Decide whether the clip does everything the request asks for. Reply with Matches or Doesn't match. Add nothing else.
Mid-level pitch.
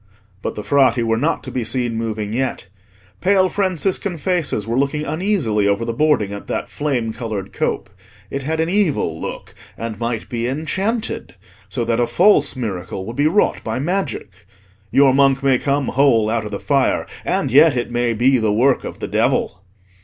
Doesn't match